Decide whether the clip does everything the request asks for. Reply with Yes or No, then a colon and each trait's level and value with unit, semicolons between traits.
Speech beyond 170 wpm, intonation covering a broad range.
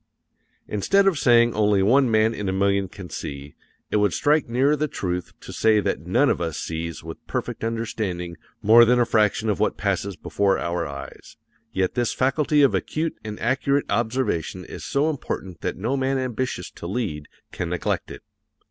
Yes: average, 185 wpm; wide, 6.1 semitones